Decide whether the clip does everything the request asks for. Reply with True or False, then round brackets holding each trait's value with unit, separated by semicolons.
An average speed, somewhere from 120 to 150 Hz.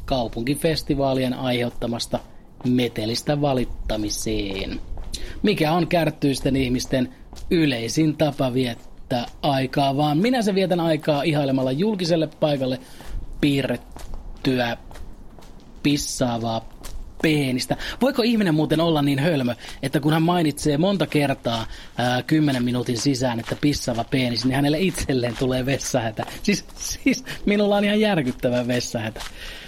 True (110 wpm; 135 Hz)